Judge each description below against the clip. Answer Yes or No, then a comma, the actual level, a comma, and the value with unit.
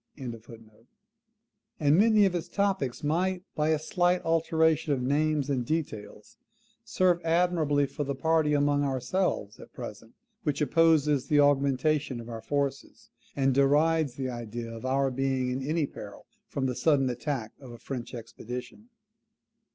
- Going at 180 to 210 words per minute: No, average, 150 wpm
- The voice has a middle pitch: Yes, medium, 145 Hz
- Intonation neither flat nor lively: Yes, average, 4.1 semitones